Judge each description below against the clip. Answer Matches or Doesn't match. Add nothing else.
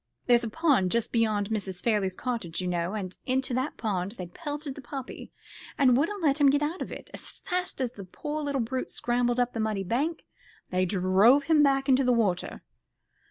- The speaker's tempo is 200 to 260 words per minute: Matches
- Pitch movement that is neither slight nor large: Doesn't match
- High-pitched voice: Matches